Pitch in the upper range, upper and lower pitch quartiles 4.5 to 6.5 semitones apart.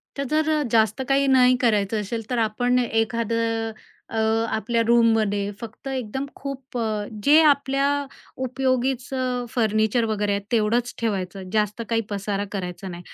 No: high, 230 Hz; average, 3.3 semitones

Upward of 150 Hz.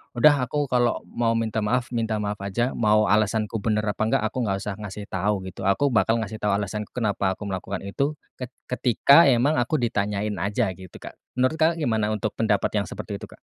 No: low, 110 Hz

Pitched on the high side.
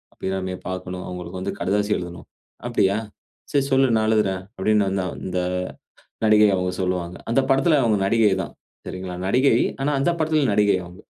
No: low, 100 Hz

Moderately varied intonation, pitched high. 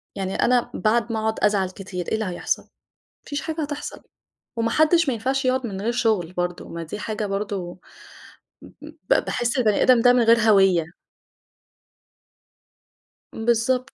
Yes: average, 4.3 semitones; high, 220 Hz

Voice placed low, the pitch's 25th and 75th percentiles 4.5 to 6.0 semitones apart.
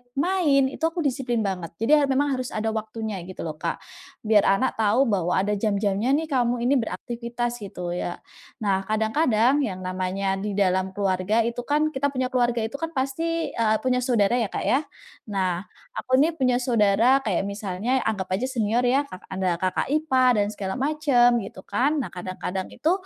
No: high, 225 Hz; average, 5.0 semitones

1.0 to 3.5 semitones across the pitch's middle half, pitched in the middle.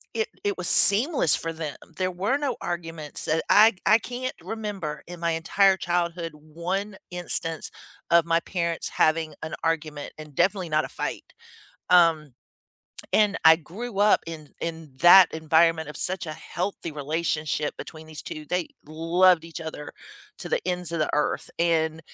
Yes: average, 2.7 semitones; medium, 165 Hz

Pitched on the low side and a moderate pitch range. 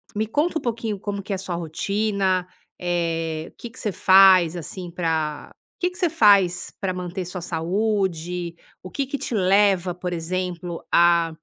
No: medium, 185 Hz; average, 3.0 semitones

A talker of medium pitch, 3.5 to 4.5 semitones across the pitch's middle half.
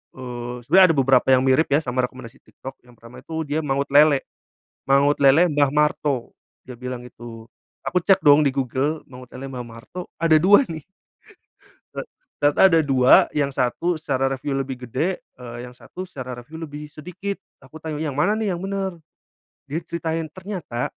Yes: medium, 145 Hz; average, 4.0 semitones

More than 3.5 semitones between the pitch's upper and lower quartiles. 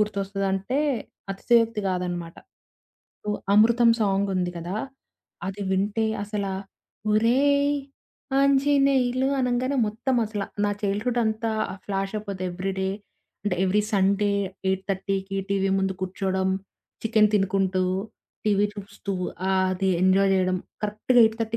No: average, 2.9 semitones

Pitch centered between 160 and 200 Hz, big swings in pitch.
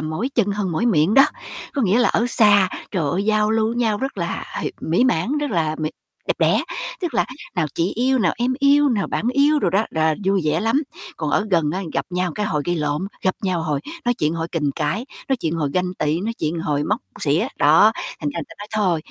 Yes: medium, 185 Hz; wide, 6.1 semitones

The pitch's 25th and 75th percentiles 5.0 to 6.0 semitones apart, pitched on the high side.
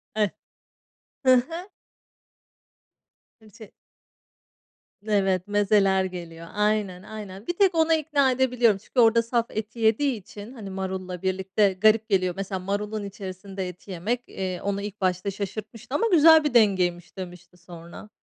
No: average, 3.5 semitones; high, 205 Hz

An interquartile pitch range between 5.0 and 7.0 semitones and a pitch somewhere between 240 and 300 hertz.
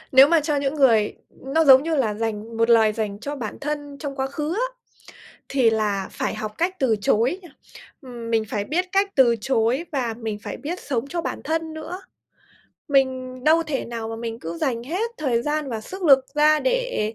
Yes: average, 5.3 semitones; very high, 265 Hz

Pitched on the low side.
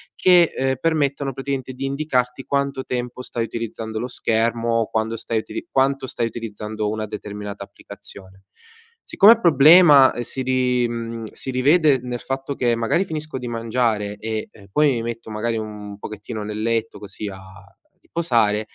Yes: low, 120 Hz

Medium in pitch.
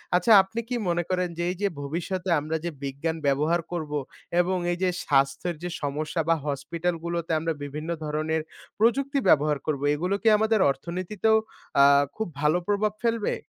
Yes: medium, 170 Hz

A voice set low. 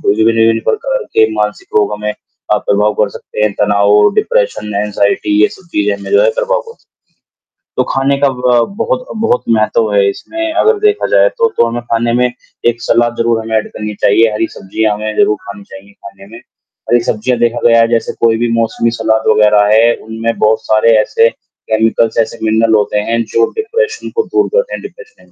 Yes: low, 115 Hz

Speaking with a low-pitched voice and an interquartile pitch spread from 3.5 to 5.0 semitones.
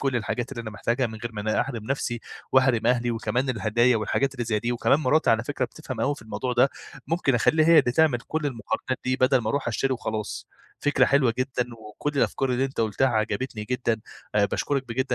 No: low, 125 Hz; average, 3.0 semitones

